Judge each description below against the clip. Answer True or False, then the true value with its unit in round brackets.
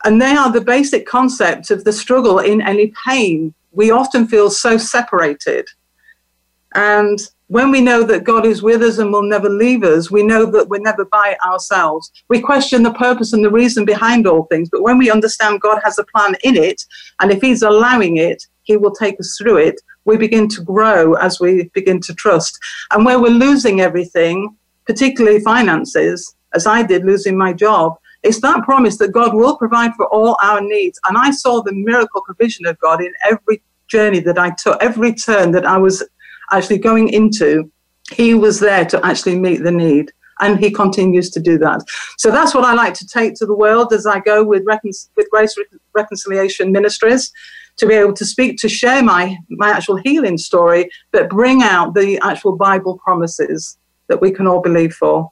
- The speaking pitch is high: True (210 Hz)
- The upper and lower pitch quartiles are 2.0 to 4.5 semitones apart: True (3.6 semitones)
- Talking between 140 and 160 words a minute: False (200 wpm)